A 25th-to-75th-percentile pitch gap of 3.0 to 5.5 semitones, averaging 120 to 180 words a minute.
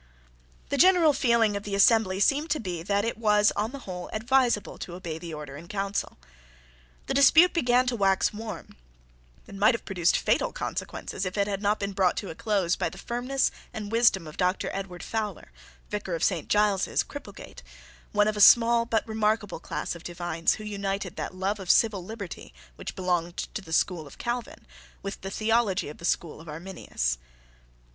No: average, 3.9 semitones; average, 190 wpm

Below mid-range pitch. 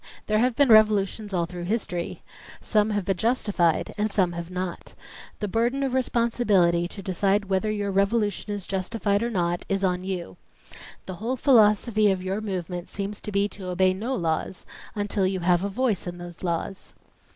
No: high, 195 Hz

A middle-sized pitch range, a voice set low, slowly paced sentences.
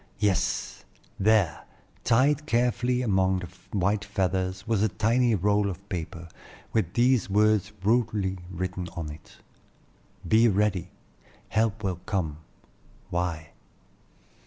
Yes: average, 3.3 semitones; low, 100 Hz; slow, 110 wpm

